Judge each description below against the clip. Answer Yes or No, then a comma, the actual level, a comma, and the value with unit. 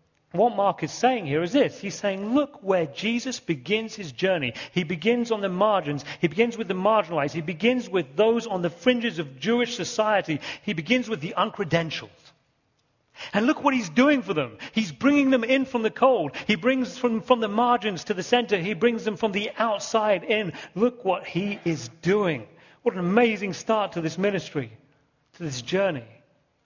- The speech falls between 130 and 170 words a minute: No, average, 195 wpm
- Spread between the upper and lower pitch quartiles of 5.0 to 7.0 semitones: Yes, average, 5.3 semitones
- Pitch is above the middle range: Yes, high, 205 Hz